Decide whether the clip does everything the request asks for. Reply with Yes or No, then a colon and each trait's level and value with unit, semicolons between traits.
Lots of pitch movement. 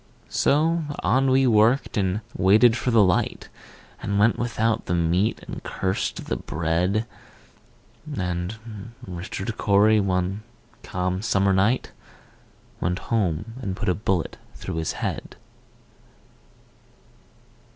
No: average, 3.7 semitones